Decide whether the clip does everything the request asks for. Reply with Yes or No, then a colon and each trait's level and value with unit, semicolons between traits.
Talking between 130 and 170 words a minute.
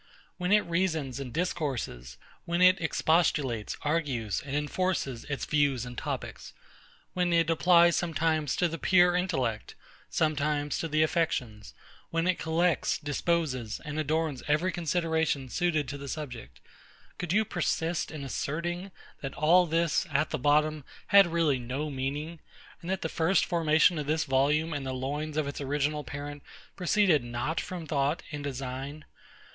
Yes: average, 150 wpm